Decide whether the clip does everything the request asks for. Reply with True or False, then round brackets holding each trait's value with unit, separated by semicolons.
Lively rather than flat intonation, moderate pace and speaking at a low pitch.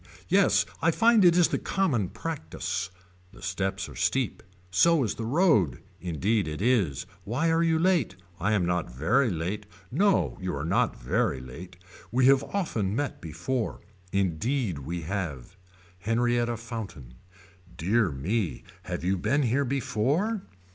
True (7.5 semitones; 150 wpm; 110 Hz)